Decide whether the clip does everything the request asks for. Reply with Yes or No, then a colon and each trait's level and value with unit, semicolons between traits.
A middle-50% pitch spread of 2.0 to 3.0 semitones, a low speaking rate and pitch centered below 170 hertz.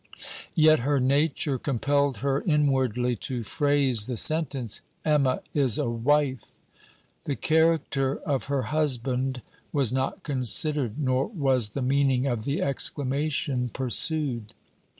Yes: narrow, 2.6 semitones; slow, 120 wpm; low, 135 Hz